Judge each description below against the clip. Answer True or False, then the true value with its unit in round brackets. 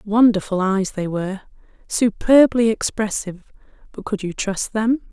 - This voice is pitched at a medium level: False (210 Hz)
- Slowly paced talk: True (130 wpm)